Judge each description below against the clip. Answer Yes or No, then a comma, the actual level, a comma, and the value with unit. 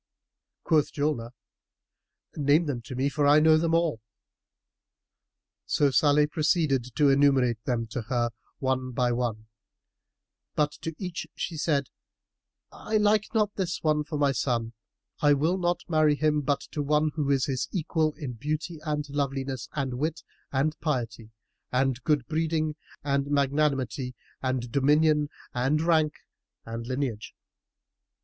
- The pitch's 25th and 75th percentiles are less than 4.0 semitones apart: Yes, average, 3.1 semitones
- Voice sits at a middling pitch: Yes, medium, 145 Hz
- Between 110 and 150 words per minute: Yes, average, 140 wpm